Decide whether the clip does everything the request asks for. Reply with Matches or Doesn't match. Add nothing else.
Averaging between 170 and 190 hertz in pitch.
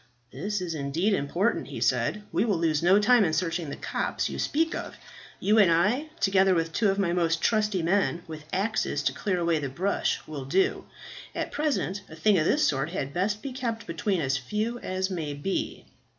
Matches